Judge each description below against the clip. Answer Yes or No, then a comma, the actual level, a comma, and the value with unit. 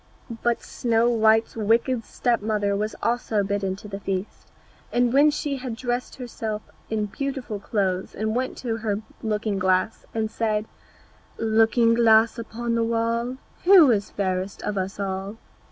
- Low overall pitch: No, high, 220 Hz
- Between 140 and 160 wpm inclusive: Yes, average, 155 wpm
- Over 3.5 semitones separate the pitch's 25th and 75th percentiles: No, narrow, 2.6 semitones